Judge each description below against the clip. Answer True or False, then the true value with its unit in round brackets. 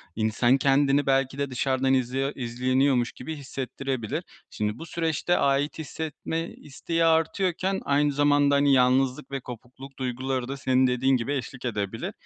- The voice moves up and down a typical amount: False (2.2 semitones)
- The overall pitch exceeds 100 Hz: True (135 Hz)